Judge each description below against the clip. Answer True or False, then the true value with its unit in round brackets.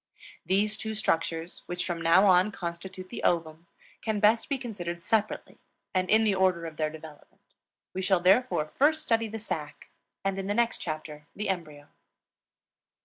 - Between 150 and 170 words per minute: True (165 wpm)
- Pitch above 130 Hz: True (185 Hz)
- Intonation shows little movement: False (4.4 semitones)